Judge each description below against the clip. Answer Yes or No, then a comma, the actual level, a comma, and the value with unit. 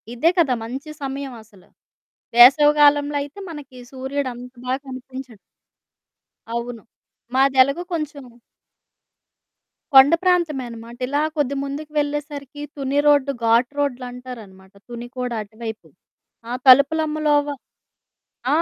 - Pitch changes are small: No, average, 3.0 semitones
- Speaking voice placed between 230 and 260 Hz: No, very high, 270 Hz